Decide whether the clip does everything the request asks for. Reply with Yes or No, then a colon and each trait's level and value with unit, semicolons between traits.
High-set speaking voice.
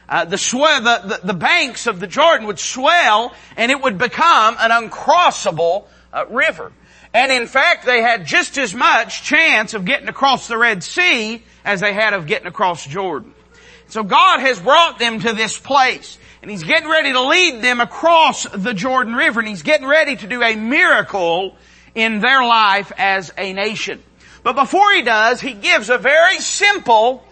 Yes: high, 245 Hz